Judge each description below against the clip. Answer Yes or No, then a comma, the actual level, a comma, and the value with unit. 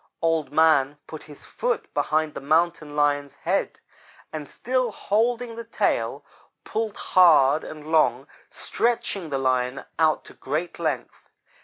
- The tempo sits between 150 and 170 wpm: No, slow, 135 wpm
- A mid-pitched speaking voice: Yes, medium, 155 Hz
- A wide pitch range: Yes, wide, 6.1 semitones